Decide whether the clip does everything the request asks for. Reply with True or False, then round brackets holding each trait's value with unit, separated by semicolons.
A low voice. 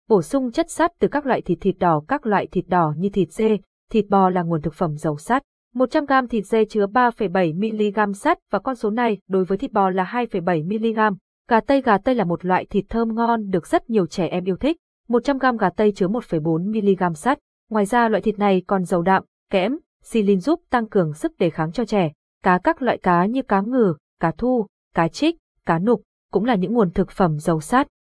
False (210 Hz)